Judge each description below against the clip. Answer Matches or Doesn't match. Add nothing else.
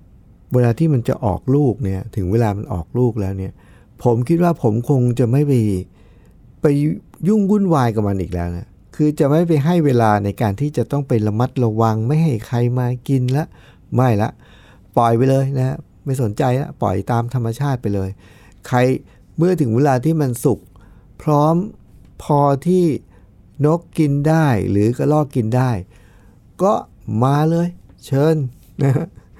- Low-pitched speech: Matches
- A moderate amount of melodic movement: Doesn't match